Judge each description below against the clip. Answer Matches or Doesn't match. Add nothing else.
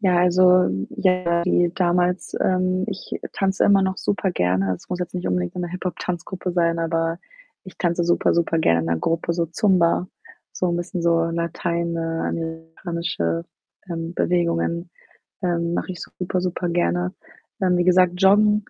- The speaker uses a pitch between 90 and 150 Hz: Doesn't match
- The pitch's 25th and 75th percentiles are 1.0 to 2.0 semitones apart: Matches